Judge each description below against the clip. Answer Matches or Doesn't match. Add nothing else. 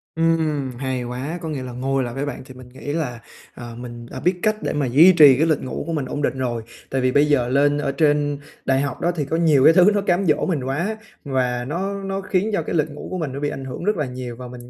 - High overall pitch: Doesn't match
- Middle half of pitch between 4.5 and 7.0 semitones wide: Doesn't match